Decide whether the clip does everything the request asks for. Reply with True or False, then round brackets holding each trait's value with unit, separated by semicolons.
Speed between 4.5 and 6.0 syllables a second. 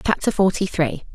True (5.4 syllables/s)